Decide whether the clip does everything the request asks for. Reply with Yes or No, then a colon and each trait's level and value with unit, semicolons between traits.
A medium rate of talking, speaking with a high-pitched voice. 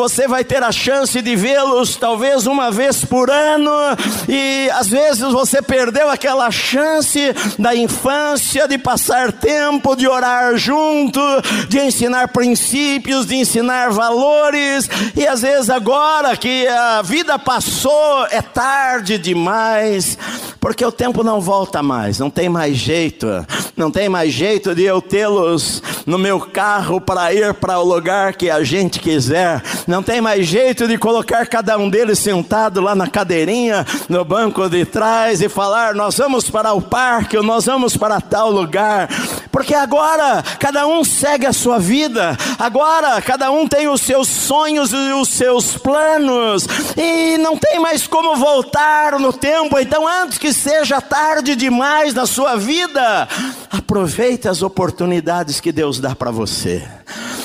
Yes: average, 150 wpm; high, 245 Hz